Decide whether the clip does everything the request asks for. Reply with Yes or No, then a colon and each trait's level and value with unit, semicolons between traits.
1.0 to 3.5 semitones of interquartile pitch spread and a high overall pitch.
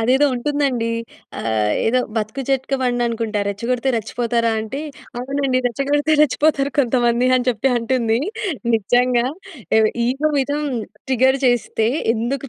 Yes: average, 2.8 semitones; high, 245 Hz